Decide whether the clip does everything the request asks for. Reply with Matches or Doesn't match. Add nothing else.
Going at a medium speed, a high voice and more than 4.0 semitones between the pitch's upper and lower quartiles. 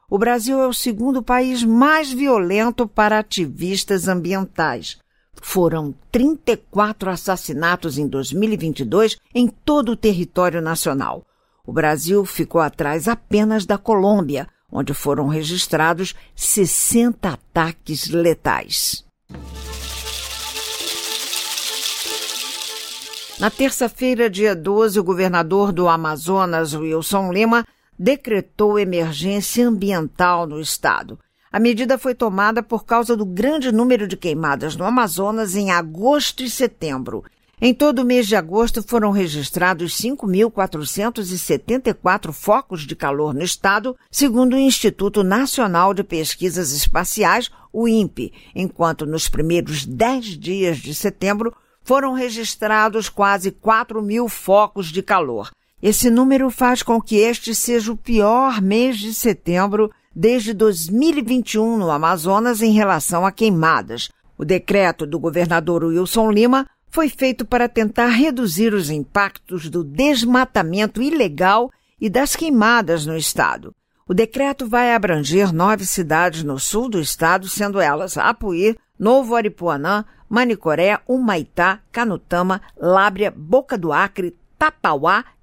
Doesn't match